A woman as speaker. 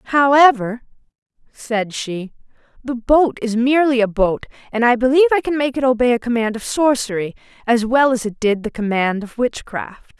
Yes: female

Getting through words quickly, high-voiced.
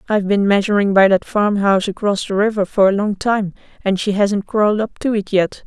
Yes: fast, 220 wpm; high, 200 Hz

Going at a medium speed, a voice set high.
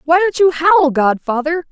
Yes: average, 175 wpm; very high, 320 Hz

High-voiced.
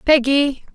Yes: very high, 275 Hz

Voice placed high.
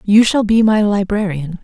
Yes: high, 205 Hz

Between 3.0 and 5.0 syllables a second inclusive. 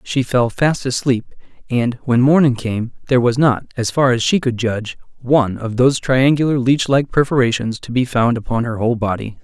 No: 5.3 syllables/s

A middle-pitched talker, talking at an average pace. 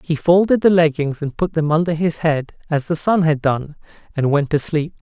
No: medium, 160 Hz; fast, 225 wpm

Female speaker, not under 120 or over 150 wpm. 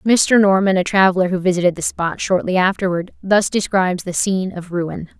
No: female; average, 185 wpm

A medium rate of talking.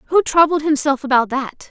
Yes: average, 175 wpm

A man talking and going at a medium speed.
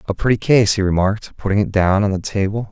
No: male; fast, 245 wpm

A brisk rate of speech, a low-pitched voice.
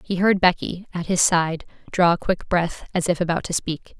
No: fast, 225 wpm; medium, 175 Hz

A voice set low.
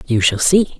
No: medium, 150 Hz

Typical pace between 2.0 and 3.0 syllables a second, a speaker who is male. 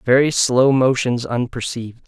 No: 4.6 syllables/s; male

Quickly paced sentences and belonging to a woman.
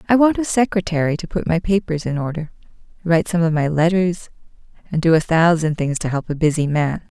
Yes: fast, 210 wpm; female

